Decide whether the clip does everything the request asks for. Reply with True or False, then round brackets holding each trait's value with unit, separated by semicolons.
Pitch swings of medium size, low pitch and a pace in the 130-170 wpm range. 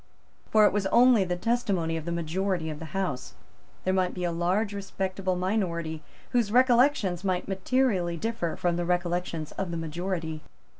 False (3.1 semitones; 185 Hz; 165 wpm)